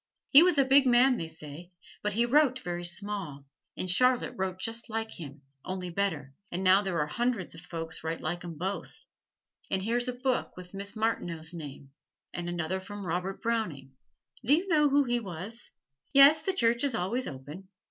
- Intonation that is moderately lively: No, wide, 5.9 semitones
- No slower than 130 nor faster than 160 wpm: No, average, 190 wpm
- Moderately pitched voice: No, high, 195 Hz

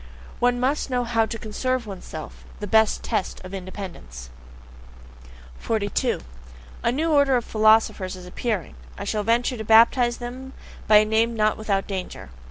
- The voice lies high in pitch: Yes, high, 220 Hz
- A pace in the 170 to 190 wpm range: No, average, 155 wpm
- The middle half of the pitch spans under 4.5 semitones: Yes, average, 3.4 semitones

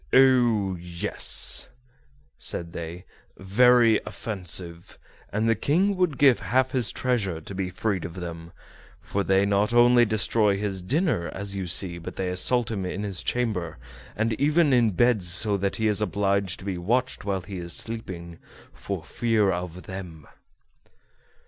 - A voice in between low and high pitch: No, low, 100 Hz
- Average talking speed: Yes, average, 155 wpm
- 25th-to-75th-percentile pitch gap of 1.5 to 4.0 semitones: No, average, 4.6 semitones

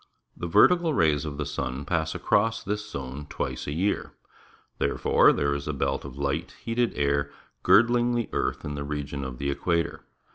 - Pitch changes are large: Yes, wide, 6.8 semitones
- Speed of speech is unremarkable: Yes, average, 180 wpm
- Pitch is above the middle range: No, very low, 75 Hz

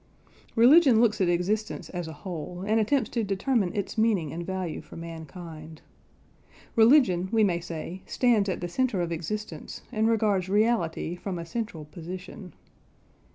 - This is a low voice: No, high, 190 Hz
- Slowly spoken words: No, average, 155 wpm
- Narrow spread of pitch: No, average, 4.4 semitones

